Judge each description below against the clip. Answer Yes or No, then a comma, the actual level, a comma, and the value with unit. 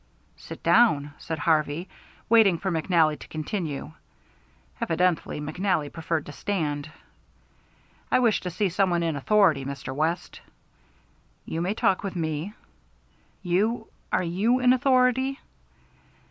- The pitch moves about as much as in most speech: Yes, average, 4.8 semitones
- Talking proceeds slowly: Yes, slow, 125 wpm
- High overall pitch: No, medium, 175 Hz